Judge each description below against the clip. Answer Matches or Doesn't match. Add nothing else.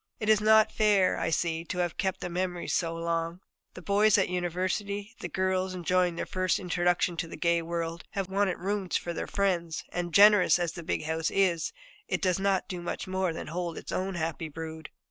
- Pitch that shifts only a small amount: Matches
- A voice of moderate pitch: Matches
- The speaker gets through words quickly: Matches